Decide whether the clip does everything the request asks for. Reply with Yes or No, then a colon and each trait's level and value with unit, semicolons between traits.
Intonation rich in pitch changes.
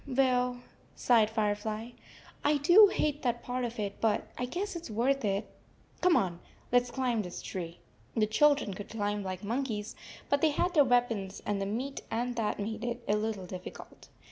No: average, 4.1 semitones